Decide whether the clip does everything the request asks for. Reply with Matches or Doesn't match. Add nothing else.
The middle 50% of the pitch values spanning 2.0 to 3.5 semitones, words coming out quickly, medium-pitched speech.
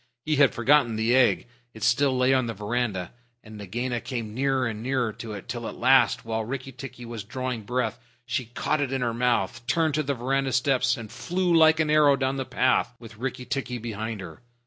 Doesn't match